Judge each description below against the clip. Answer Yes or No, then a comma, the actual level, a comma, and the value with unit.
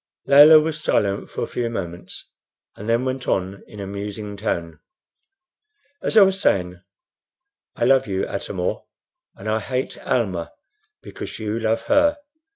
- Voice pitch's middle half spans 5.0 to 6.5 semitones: Yes, average, 5.3 semitones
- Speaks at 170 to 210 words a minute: No, average, 155 wpm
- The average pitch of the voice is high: No, low, 110 Hz